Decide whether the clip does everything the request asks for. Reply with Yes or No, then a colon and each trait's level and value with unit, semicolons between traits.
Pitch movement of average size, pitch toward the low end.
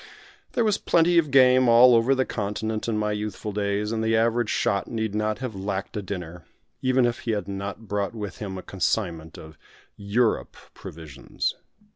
Yes: average, 3.1 semitones; low, 105 Hz